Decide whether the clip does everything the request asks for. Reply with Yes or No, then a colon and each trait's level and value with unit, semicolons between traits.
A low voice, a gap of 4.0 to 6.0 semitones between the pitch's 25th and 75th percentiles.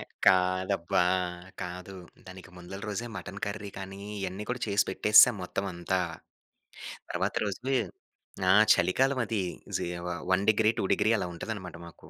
No: very low, 95 Hz; narrow, 2.5 semitones